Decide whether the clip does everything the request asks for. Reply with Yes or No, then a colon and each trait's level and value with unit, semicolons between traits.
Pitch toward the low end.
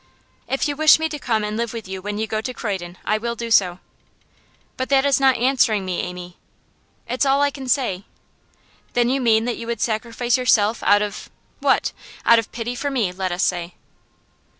No: high, 230 Hz